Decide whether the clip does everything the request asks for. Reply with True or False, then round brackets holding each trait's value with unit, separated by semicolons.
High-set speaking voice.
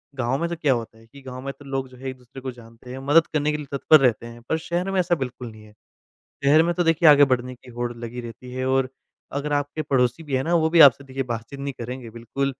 False (135 Hz)